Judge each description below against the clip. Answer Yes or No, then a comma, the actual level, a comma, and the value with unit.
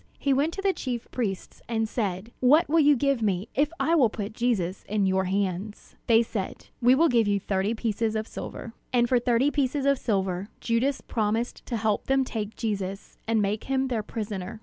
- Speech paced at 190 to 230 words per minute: Yes, average, 200 wpm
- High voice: Yes, high, 225 Hz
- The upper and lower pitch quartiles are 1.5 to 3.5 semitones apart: No, average, 4.1 semitones